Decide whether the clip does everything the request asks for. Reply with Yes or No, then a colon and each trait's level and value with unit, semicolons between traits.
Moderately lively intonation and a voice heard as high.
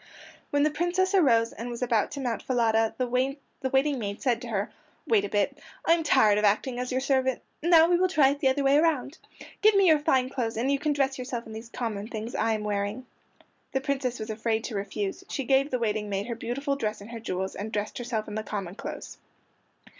Yes: average, 4.1 semitones; high, 245 Hz